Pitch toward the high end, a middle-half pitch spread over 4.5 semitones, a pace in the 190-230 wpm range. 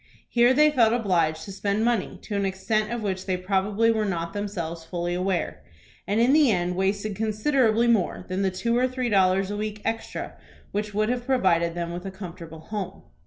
No: high, 200 Hz; average, 3.6 semitones; average, 200 wpm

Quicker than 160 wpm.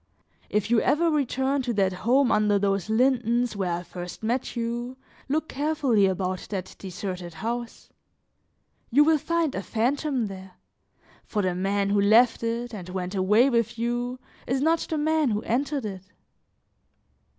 No: average, 155 wpm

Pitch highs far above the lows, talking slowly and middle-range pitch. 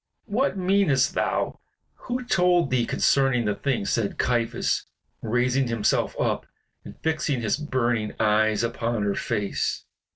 No: wide, 5.7 semitones; slow, 130 wpm; low, 125 Hz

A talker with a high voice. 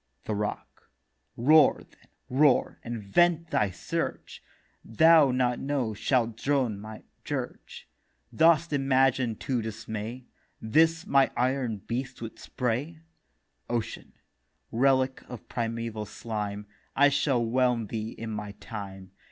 No: low, 120 Hz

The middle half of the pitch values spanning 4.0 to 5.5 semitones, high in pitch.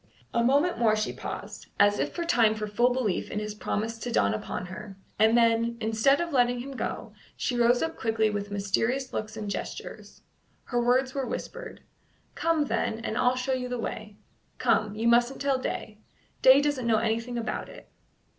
No: average, 3.0 semitones; high, 235 Hz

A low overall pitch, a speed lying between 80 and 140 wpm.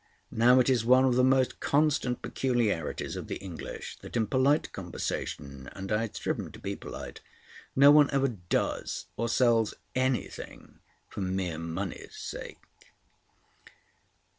Yes: low, 120 Hz; slow, 135 wpm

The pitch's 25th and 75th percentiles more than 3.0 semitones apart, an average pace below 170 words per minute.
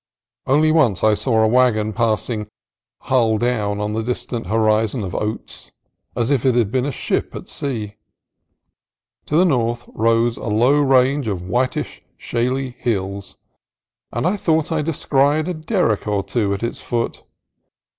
Yes: average, 3.9 semitones; average, 155 wpm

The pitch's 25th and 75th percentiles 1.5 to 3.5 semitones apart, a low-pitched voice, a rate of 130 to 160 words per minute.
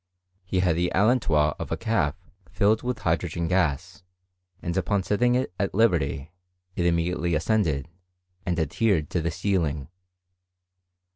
No: average, 4.1 semitones; very low, 90 Hz; slow, 135 wpm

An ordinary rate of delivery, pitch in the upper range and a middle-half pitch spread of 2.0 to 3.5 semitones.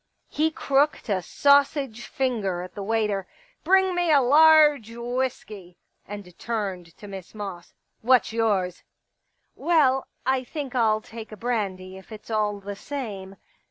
No: average, 170 wpm; high, 225 Hz; wide, 5.5 semitones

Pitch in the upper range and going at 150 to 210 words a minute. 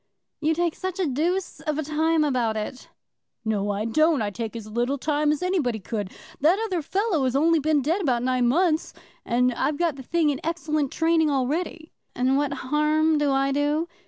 Yes: very high, 295 Hz; average, 195 wpm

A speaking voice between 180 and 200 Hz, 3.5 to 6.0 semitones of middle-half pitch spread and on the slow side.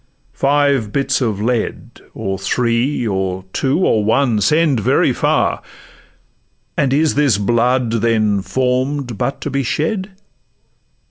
No: low, 125 Hz; average, 4.4 semitones; slow, 125 wpm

